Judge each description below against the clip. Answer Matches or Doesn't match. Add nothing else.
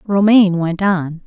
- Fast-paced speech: Doesn't match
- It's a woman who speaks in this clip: Matches